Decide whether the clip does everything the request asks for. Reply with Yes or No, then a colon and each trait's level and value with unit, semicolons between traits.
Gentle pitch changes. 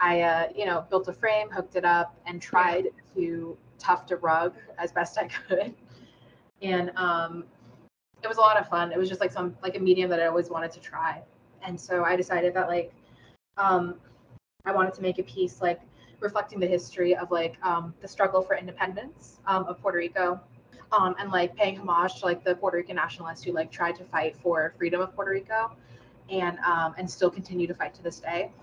Yes: narrow, 1.6 semitones